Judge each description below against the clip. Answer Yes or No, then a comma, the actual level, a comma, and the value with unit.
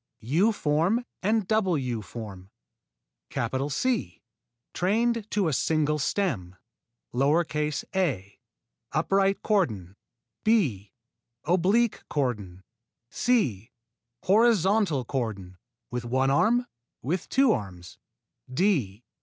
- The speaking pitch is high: No, medium, 150 Hz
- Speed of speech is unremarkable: No, slow, 90 wpm